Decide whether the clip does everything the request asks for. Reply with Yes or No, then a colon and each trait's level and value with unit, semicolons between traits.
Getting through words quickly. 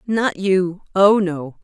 No: slow, 110 wpm